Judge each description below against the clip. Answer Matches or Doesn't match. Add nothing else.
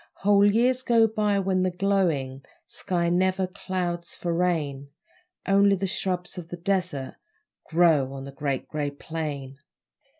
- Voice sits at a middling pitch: Matches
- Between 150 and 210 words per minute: Doesn't match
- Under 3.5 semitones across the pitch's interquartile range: Doesn't match